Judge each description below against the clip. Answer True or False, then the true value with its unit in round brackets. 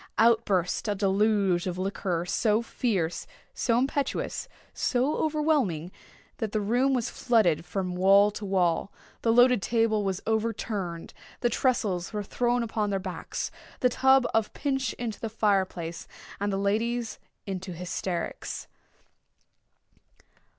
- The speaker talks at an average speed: False (115 wpm)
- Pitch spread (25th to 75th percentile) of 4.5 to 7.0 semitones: False (4.1 semitones)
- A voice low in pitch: False (210 Hz)